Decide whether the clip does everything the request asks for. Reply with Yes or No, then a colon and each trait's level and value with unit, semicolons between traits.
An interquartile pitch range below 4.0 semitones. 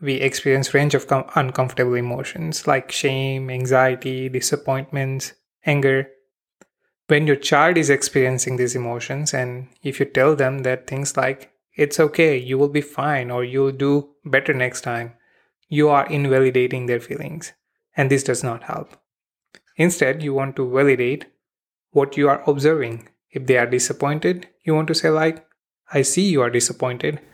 Yes: narrow, 2.4 semitones